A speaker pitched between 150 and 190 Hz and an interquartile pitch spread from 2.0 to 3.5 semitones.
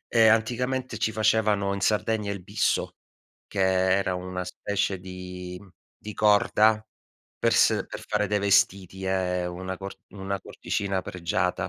No: low, 100 Hz; narrow, 2.5 semitones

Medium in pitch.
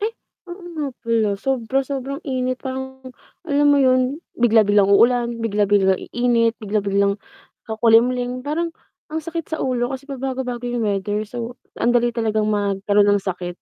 No: high, 240 Hz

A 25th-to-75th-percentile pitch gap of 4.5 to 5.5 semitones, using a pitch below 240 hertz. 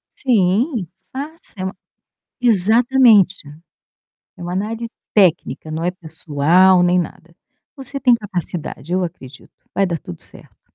Yes: average, 5.1 semitones; medium, 185 Hz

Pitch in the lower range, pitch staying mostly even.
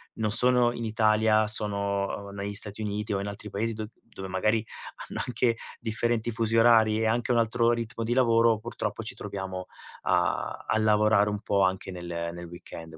Yes: low, 110 Hz; narrow, 2.3 semitones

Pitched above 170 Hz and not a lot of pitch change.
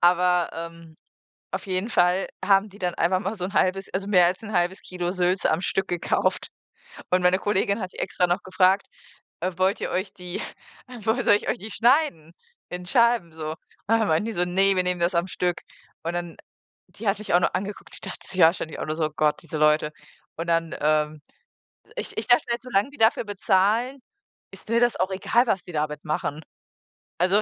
No: medium, 185 Hz; average, 3.0 semitones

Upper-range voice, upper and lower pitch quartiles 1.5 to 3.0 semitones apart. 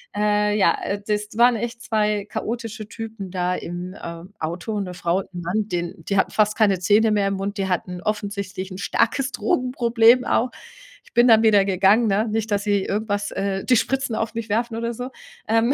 Yes: high, 210 Hz; narrow, 2.6 semitones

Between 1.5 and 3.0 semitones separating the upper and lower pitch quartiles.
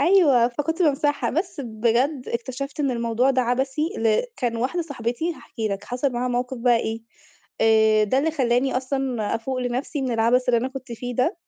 Yes: average, 2.7 semitones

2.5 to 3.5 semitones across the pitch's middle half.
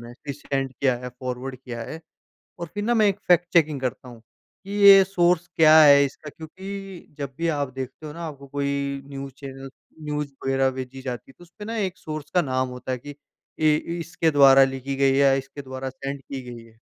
No: average, 4.0 semitones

